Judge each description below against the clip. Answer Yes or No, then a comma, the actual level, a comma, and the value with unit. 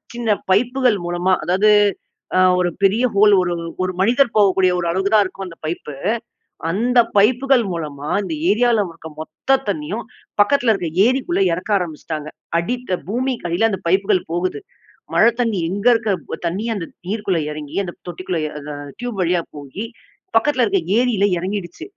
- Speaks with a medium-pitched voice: No, high, 195 Hz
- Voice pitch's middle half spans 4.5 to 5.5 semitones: Yes, average, 4.9 semitones